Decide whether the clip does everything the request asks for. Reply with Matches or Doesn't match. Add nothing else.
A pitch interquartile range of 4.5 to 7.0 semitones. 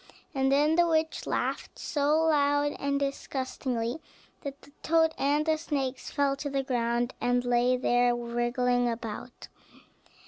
Doesn't match